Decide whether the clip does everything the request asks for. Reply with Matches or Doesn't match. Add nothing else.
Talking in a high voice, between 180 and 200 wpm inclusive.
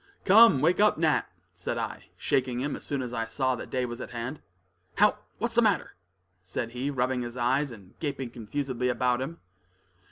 Doesn't match